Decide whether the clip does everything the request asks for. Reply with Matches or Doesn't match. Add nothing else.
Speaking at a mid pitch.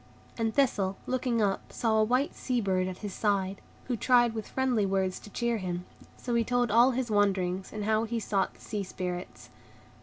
Doesn't match